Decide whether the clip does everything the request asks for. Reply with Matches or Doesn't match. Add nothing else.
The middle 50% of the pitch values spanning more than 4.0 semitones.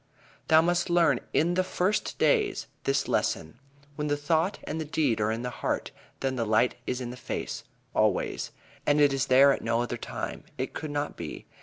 Matches